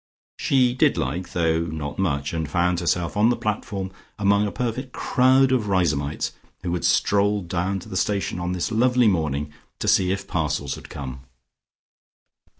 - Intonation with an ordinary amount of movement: Yes, average, 4.4 semitones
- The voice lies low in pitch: Yes, very low, 90 Hz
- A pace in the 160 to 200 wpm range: Yes, average, 165 wpm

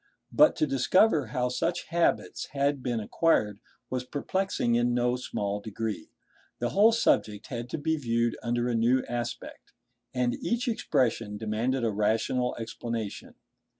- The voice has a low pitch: Yes, low, 120 Hz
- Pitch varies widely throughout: No, average, 3.6 semitones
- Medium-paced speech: Yes, average, 145 wpm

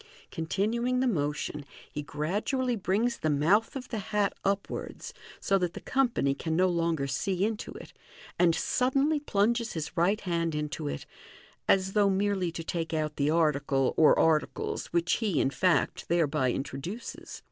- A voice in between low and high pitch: Yes, medium, 175 Hz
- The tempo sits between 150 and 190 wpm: Yes, average, 160 wpm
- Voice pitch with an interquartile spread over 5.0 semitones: Yes, wide, 5.5 semitones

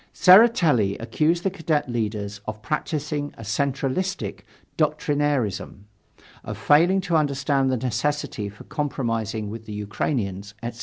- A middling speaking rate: No, slow, 120 wpm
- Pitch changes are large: Yes, wide, 5.8 semitones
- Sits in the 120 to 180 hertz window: Yes, low, 135 Hz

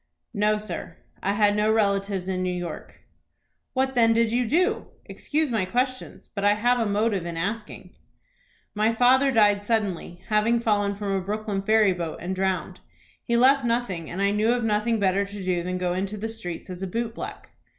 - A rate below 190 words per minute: No, average, 195 wpm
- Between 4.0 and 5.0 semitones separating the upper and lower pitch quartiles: No, average, 3.1 semitones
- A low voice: No, high, 210 Hz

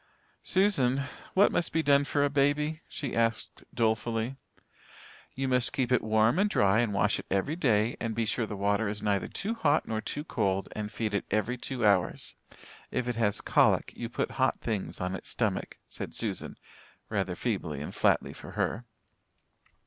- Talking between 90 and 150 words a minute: No, average, 180 wpm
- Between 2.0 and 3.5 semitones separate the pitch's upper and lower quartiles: No, average, 4.9 semitones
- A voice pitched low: Yes, low, 115 Hz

